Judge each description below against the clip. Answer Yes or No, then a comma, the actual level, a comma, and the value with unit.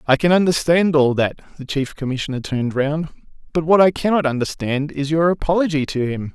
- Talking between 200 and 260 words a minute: No, average, 170 wpm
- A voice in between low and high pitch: Yes, medium, 150 Hz